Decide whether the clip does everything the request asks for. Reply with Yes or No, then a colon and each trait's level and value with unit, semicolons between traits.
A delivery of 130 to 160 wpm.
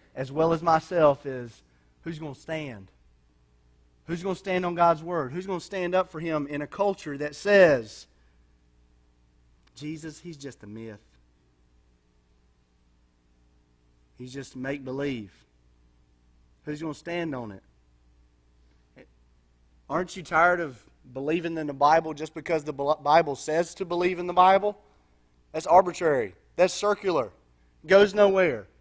Yes: average, 140 wpm